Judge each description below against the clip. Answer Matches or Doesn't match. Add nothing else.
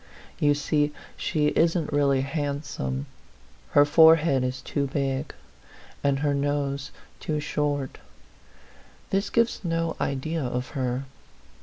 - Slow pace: Matches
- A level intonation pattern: Matches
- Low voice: Doesn't match